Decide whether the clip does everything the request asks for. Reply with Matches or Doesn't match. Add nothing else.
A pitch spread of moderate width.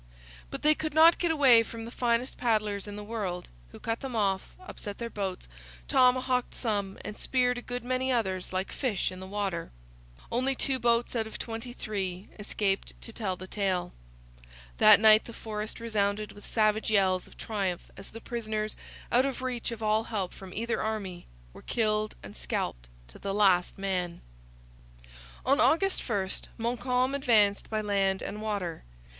Matches